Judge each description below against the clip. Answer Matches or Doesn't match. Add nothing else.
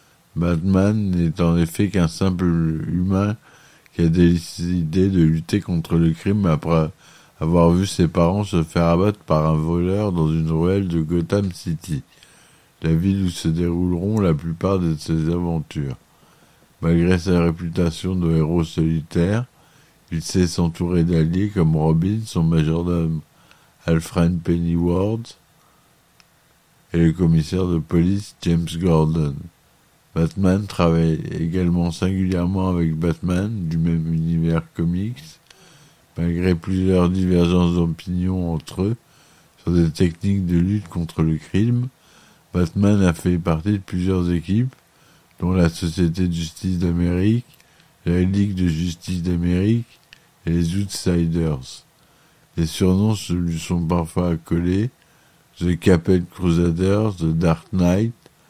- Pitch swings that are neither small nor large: Doesn't match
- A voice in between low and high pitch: Doesn't match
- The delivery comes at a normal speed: Doesn't match